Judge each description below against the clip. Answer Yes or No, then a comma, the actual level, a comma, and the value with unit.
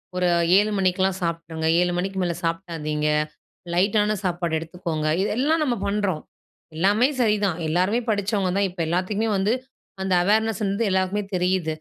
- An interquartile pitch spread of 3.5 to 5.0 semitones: No, average, 3.1 semitones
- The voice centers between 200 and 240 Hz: No, high, 190 Hz